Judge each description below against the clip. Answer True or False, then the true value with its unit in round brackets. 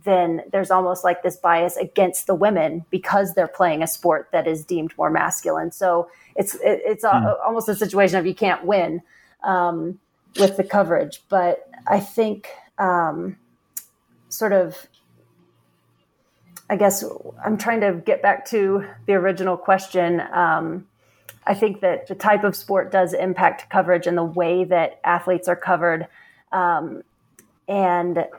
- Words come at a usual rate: True (150 wpm)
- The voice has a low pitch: False (185 Hz)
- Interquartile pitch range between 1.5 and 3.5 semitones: True (2.5 semitones)